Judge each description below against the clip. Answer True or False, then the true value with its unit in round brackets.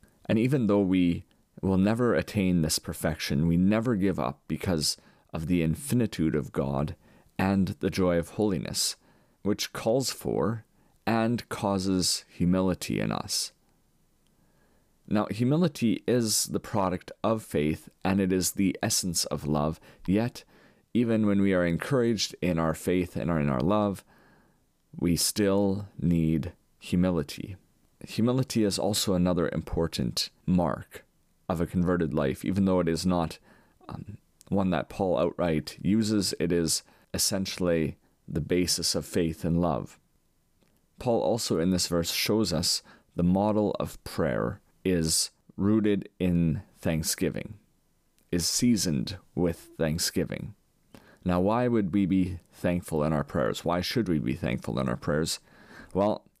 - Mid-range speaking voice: False (90 Hz)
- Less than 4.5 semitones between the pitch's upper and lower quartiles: True (3.3 semitones)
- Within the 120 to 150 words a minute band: True (140 wpm)